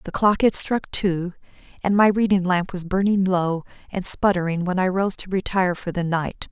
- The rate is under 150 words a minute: No, fast, 205 wpm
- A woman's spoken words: Yes, female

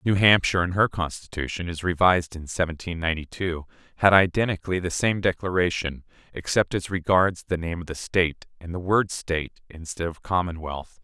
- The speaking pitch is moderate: No, very low, 90 Hz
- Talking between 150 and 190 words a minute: Yes, average, 170 wpm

